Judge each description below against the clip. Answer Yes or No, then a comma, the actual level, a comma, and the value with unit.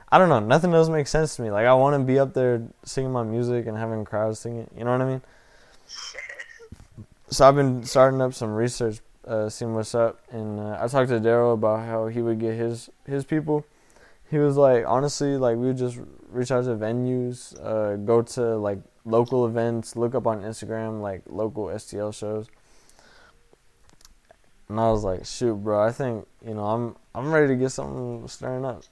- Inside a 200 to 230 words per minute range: Yes, fast, 205 wpm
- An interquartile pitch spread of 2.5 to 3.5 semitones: Yes, average, 2.9 semitones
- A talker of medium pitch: No, low, 115 Hz